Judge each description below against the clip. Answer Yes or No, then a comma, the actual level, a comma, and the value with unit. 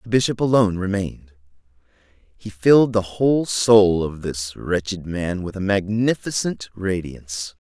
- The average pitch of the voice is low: Yes, low, 100 Hz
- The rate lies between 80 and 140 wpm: Yes, slow, 135 wpm